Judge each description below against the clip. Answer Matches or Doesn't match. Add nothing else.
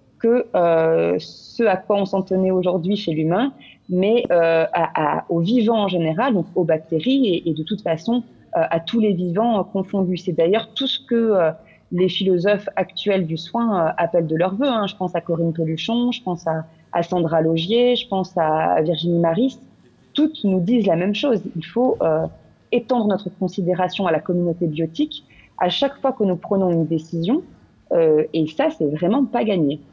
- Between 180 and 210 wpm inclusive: Matches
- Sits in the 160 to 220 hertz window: Matches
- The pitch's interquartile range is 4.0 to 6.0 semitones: Matches